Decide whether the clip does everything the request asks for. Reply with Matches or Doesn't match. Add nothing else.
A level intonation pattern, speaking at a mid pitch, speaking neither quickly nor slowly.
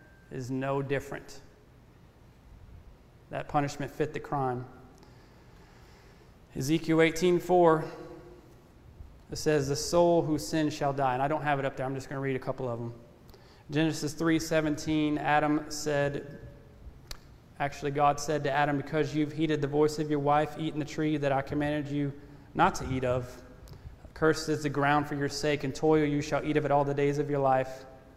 Matches